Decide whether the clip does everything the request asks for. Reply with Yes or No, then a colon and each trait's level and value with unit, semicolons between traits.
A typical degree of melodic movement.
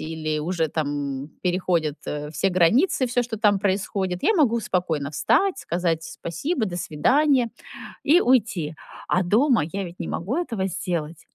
No: wide, 6.5 semitones